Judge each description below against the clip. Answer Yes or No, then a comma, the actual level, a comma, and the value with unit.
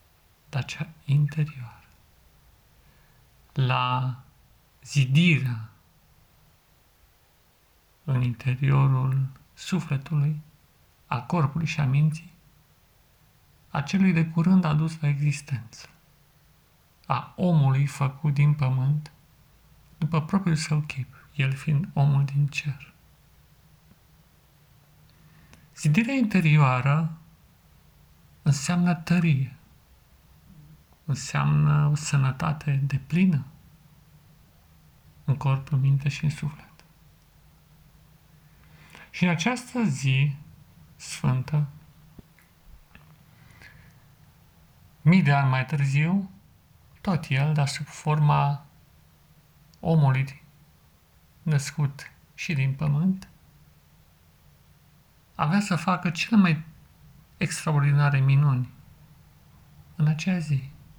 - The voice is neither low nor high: Yes, medium, 145 Hz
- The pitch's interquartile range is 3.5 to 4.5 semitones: No, narrow, 2.6 semitones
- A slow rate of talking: Yes, slow, 80 wpm